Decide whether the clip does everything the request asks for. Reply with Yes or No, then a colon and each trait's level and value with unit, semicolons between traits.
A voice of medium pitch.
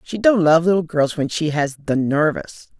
Yes: medium, 160 Hz